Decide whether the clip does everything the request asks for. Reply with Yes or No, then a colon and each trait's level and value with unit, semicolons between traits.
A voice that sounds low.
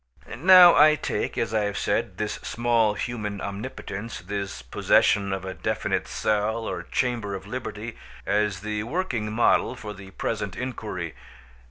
Yes: low, 105 Hz